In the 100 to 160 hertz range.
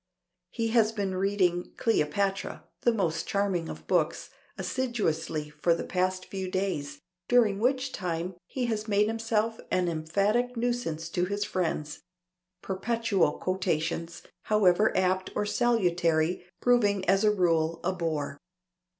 No: high, 190 Hz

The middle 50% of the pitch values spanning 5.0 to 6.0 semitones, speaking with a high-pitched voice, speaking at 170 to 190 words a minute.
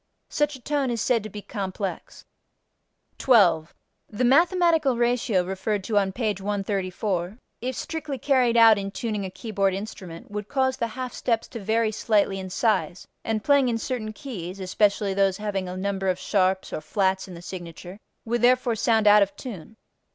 No: average, 3.9 semitones; high, 210 Hz; average, 175 wpm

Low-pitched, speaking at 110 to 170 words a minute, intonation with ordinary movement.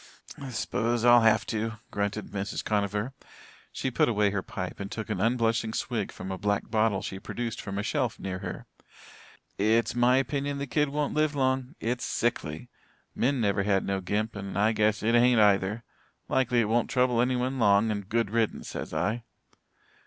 No: low, 110 Hz; average, 180 wpm; average, 3.2 semitones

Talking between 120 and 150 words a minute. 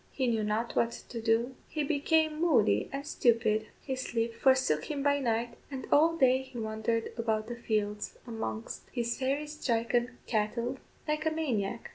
No: average, 165 wpm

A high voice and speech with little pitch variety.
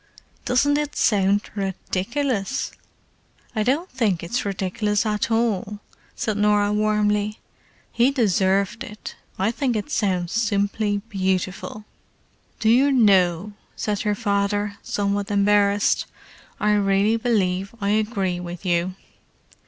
Yes: high, 205 Hz; narrow, 2.1 semitones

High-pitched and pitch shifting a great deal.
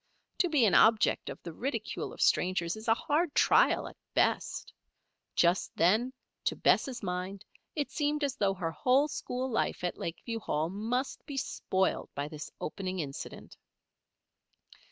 Yes: high, 215 Hz; wide, 6.6 semitones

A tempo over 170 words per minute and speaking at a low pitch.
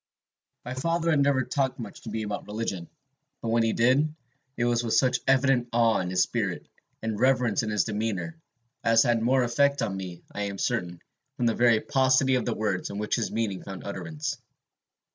Yes: average, 200 wpm; low, 115 Hz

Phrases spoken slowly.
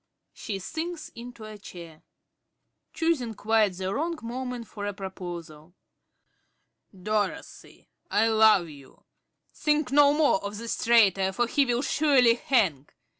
Yes: slow, 130 wpm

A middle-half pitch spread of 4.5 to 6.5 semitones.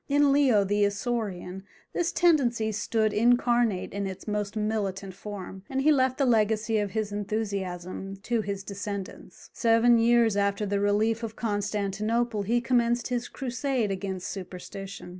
No: average, 3.1 semitones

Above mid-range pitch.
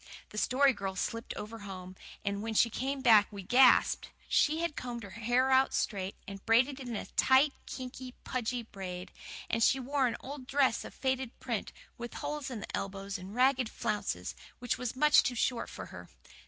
Yes: high, 240 Hz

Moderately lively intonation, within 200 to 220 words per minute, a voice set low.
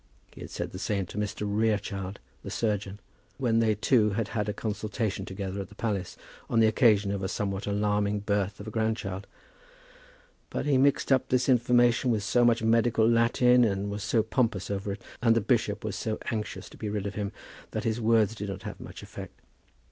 No: narrow, 2.2 semitones; fast, 205 wpm; low, 105 Hz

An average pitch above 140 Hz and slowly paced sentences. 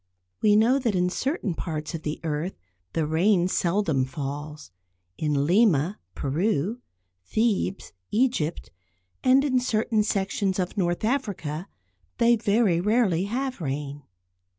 Yes: high, 190 Hz; slow, 125 wpm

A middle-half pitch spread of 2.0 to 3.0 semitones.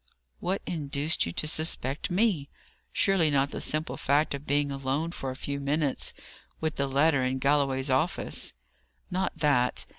Yes: narrow, 2.6 semitones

